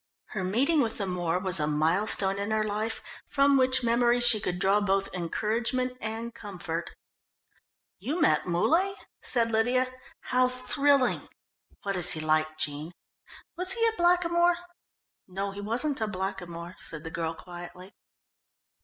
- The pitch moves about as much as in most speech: No, wide, 6.0 semitones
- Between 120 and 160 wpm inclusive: Yes, average, 145 wpm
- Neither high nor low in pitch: No, high, 210 Hz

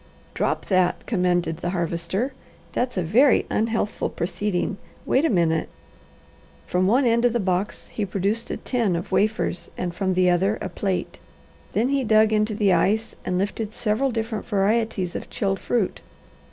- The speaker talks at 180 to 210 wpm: No, average, 165 wpm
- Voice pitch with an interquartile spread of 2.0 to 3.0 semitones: No, average, 3.7 semitones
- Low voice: No, high, 205 Hz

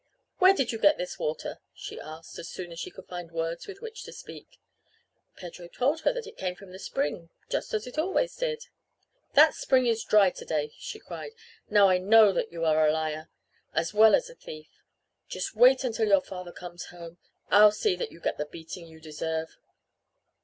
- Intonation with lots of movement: Yes, wide, 7.0 semitones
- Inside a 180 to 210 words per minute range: Yes, fast, 205 wpm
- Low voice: No, medium, 185 Hz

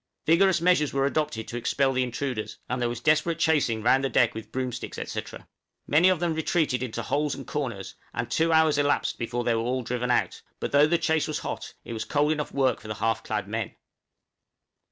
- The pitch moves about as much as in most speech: Yes, average, 4.4 semitones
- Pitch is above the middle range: No, low, 135 Hz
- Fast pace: Yes, fast, 215 wpm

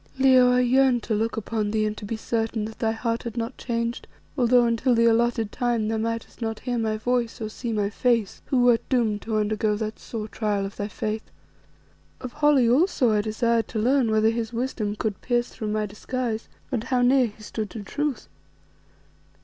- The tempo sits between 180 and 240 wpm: Yes, average, 200 wpm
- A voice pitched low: No, high, 230 Hz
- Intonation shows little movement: Yes, narrow, 2.3 semitones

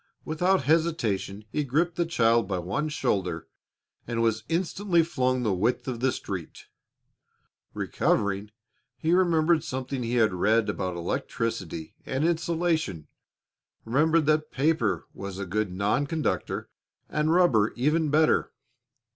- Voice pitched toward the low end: Yes, low, 130 Hz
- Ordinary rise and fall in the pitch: No, wide, 7.5 semitones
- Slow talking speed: Yes, slow, 130 wpm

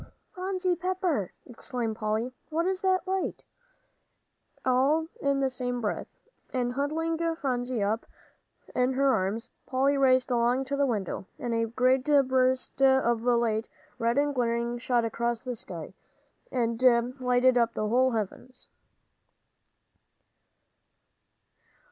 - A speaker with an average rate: No, slow, 120 wpm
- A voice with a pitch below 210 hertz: No, very high, 255 Hz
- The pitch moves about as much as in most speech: Yes, average, 3.0 semitones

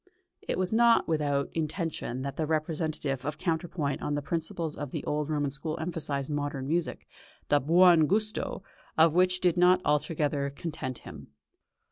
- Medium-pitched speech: Yes, medium, 155 Hz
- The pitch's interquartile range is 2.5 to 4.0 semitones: Yes, average, 3.0 semitones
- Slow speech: No, average, 155 wpm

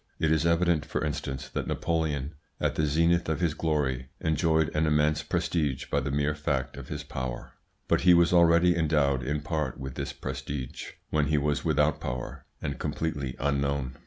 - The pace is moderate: Yes, average, 180 wpm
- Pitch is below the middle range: Yes, very low, 75 Hz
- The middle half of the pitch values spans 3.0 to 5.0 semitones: No, narrow, 2.5 semitones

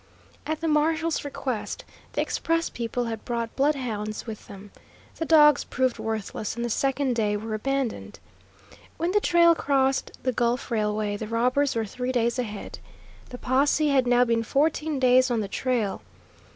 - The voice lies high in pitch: Yes, very high, 250 Hz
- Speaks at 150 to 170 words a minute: Yes, average, 165 wpm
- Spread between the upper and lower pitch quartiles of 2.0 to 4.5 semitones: Yes, average, 4.0 semitones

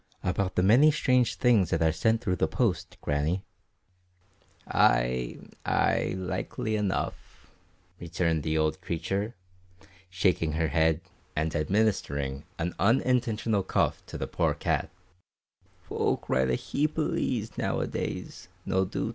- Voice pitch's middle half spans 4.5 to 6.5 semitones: Yes, wide, 5.6 semitones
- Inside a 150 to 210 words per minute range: No, slow, 135 wpm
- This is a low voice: Yes, very low, 90 Hz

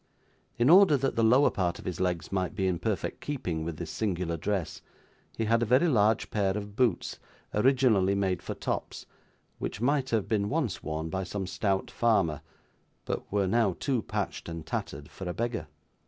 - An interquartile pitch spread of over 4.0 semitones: Yes, average, 4.7 semitones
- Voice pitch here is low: Yes, low, 100 Hz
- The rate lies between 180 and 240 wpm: Yes, average, 185 wpm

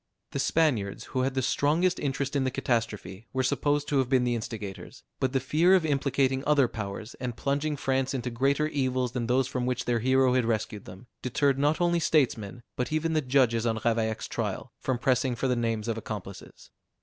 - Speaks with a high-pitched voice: No, low, 130 Hz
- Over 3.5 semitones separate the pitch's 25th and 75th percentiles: No, average, 3.1 semitones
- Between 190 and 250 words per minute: Yes, average, 200 wpm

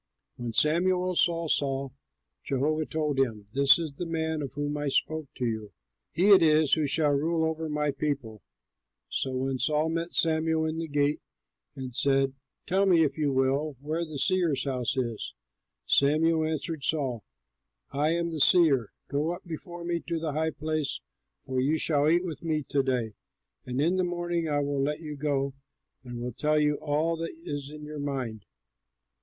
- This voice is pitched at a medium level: Yes, medium, 150 Hz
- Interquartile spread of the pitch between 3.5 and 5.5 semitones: No, average, 3.0 semitones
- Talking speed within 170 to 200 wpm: Yes, average, 180 wpm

